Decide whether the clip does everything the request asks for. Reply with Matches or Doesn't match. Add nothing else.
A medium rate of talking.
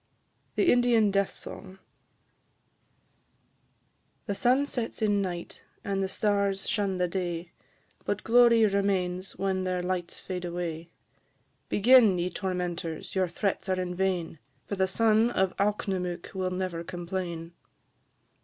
Doesn't match